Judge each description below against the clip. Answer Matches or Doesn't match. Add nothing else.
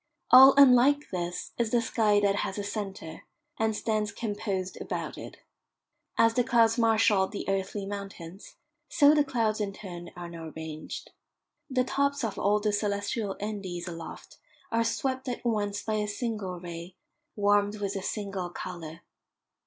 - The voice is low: Doesn't match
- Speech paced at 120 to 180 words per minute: Matches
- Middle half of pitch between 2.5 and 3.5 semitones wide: Matches